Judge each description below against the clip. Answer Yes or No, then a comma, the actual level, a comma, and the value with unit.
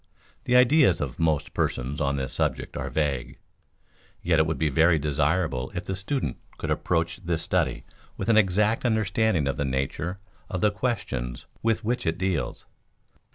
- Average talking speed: Yes, average, 165 wpm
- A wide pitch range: Yes, wide, 6.7 semitones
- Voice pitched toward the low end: Yes, very low, 85 Hz